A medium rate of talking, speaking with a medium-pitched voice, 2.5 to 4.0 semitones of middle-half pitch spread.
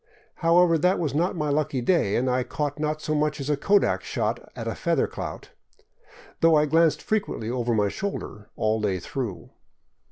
No: average, 190 wpm; medium, 150 Hz; average, 5.3 semitones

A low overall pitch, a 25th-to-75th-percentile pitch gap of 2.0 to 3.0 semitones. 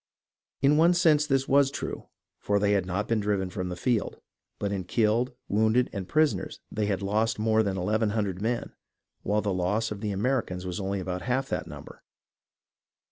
No: low, 105 Hz; average, 3.9 semitones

